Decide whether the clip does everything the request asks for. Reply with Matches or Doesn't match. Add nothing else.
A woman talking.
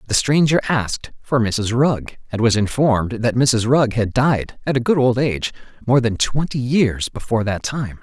Doesn't match